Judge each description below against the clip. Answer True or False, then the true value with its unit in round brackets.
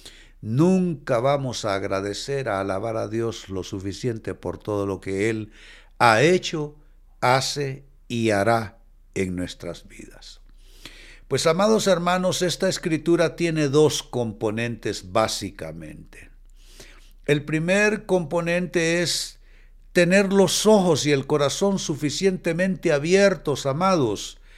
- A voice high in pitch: False (145 Hz)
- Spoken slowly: True (110 wpm)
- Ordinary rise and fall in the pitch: False (8.0 semitones)